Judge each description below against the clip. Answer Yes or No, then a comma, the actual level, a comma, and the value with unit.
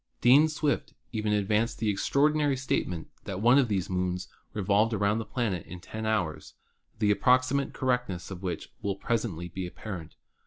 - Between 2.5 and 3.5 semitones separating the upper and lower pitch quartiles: No, average, 4.9 semitones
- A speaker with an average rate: Yes, average, 170 wpm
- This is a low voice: Yes, low, 105 Hz